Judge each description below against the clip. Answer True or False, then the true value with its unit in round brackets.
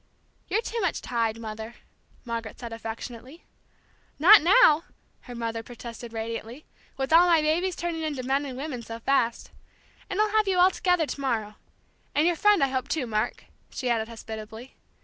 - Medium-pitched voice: False (260 Hz)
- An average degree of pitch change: False (6.5 semitones)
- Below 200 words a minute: True (170 wpm)